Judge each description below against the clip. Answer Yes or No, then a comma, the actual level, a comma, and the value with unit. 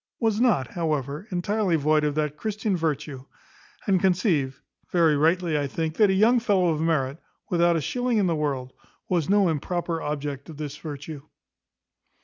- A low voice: No, medium, 165 Hz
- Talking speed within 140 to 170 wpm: Yes, average, 165 wpm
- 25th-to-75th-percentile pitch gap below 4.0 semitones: No, average, 4.3 semitones